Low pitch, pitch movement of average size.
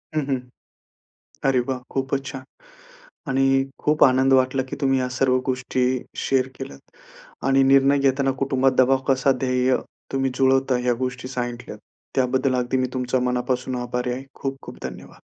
No: low, 130 Hz; narrow, 1.0 semitones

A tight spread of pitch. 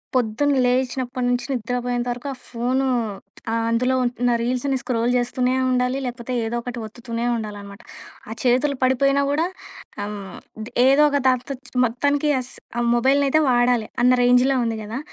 Yes: narrow, 1.7 semitones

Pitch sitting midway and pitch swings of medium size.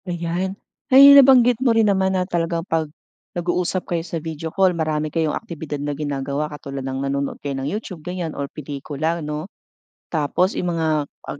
Yes: medium, 165 Hz; average, 3.7 semitones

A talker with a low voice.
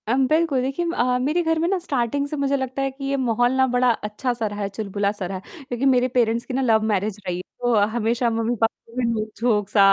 No: high, 245 Hz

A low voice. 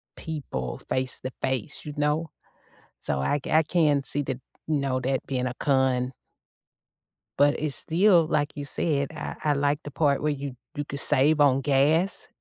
No: medium, 145 Hz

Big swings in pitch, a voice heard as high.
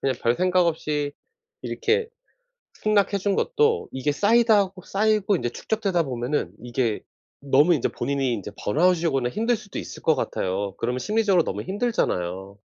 No: wide, 8.7 semitones; medium, 170 Hz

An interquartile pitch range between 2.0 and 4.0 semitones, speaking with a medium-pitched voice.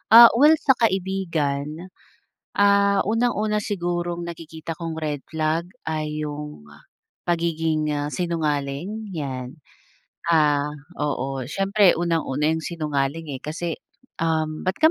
Yes: average, 3.4 semitones; medium, 165 Hz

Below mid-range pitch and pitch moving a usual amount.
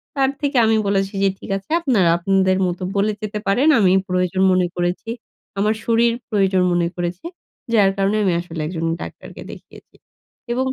No: high, 195 Hz; average, 3.1 semitones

